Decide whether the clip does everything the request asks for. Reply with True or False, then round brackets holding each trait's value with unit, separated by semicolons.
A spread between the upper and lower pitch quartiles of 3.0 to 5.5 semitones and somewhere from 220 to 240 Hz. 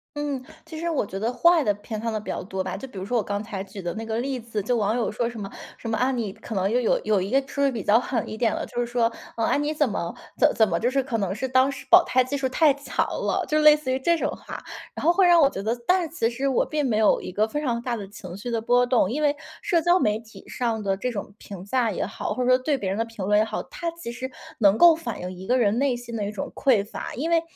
True (4.6 semitones; 235 Hz)